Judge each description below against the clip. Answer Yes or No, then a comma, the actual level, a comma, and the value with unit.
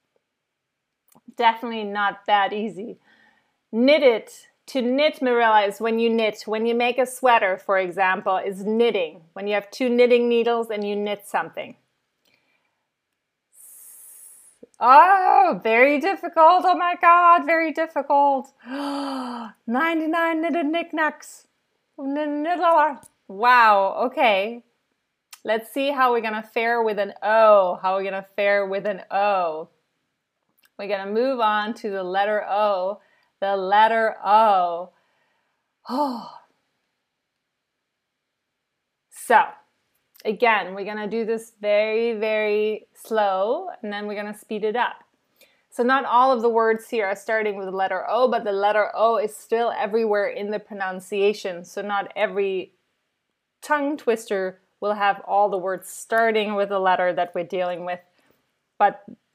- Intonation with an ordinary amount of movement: Yes, average, 4.4 semitones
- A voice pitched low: No, high, 220 Hz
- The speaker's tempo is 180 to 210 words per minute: No, slow, 135 wpm